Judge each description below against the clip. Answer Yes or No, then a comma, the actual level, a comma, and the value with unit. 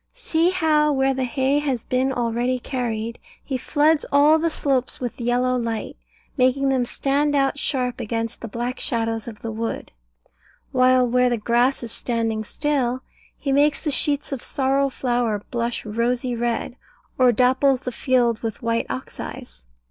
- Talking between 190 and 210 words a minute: No, average, 160 wpm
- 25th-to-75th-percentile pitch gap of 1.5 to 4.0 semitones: Yes, average, 2.8 semitones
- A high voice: Yes, very high, 250 Hz